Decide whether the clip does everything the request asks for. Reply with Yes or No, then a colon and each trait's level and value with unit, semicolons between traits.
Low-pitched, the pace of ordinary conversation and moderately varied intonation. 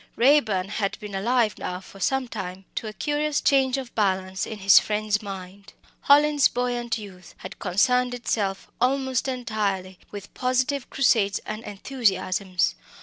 No: high, 215 Hz; average, 145 wpm; average, 4.6 semitones